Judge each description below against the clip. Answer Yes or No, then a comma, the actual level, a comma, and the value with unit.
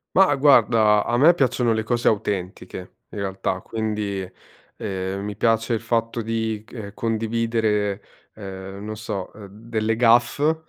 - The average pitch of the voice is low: Yes, low, 110 Hz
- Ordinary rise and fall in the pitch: No, narrow, 2.3 semitones